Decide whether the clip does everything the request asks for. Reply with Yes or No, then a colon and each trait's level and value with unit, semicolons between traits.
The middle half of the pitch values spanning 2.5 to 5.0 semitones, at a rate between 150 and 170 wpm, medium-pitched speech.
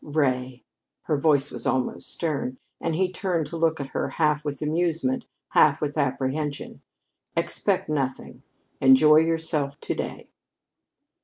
No: average, 3.0 semitones; slow, 135 wpm; medium, 150 Hz